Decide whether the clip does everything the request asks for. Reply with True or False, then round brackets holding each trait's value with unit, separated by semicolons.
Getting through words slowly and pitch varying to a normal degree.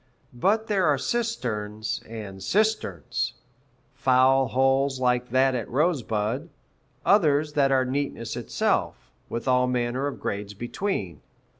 True (120 wpm; 4.0 semitones)